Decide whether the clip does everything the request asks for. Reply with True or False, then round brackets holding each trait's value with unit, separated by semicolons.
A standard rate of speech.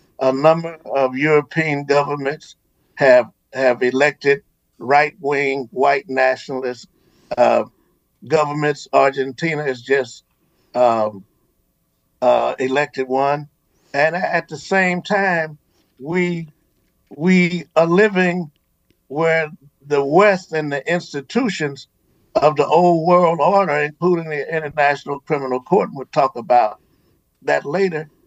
False (105 wpm)